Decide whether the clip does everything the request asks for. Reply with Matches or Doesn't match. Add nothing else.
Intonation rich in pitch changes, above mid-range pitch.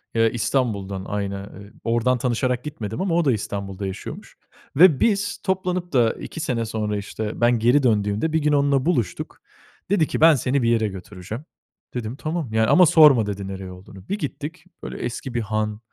Doesn't match